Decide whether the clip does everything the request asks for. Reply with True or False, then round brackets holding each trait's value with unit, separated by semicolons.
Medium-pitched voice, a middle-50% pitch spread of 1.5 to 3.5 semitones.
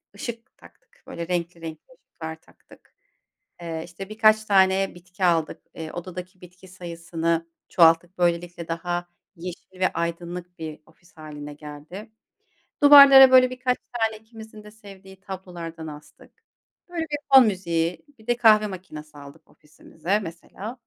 False (180 Hz; 4.3 semitones)